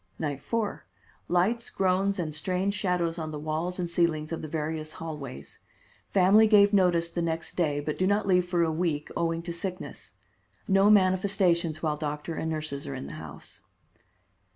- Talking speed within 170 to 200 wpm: Yes, average, 175 wpm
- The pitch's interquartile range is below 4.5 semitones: Yes, average, 3.3 semitones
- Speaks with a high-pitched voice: No, medium, 170 Hz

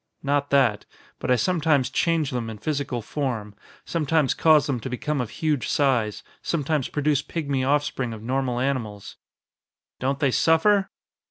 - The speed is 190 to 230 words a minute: No, average, 150 wpm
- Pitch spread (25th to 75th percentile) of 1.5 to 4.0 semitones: Yes, average, 3.4 semitones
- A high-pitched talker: No, medium, 140 Hz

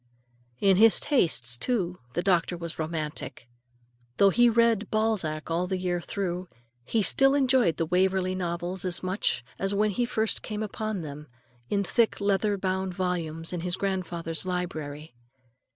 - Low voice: No, medium, 185 Hz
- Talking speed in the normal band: Yes, average, 155 wpm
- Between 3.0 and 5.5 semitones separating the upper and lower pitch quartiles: Yes, average, 3.5 semitones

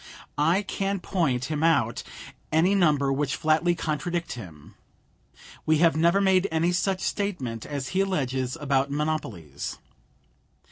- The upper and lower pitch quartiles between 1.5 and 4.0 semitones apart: No, average, 4.9 semitones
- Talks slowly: Yes, slow, 130 wpm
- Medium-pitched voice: Yes, medium, 155 Hz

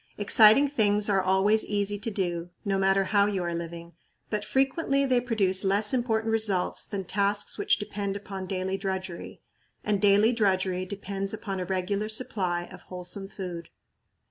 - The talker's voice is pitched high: Yes, high, 200 Hz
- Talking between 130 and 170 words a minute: Yes, average, 160 wpm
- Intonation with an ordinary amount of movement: No, narrow, 2.2 semitones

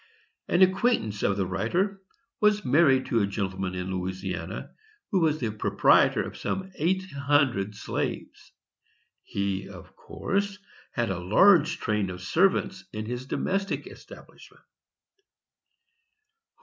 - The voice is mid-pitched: No, low, 120 Hz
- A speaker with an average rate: No, slow, 125 wpm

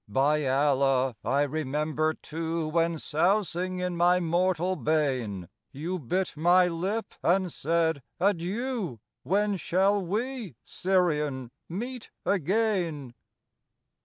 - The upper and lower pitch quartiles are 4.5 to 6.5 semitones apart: No, average, 4.0 semitones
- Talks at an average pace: No, slow, 105 wpm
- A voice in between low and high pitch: Yes, medium, 170 Hz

